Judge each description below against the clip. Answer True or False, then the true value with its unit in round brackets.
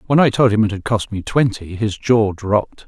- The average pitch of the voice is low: True (110 Hz)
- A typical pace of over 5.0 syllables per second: True (5.2 syllables/s)